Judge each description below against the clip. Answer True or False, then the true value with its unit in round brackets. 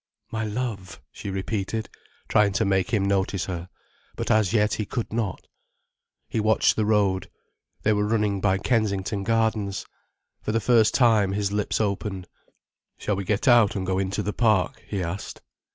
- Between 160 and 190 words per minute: True (170 wpm)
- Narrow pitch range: True (2.1 semitones)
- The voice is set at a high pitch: False (105 Hz)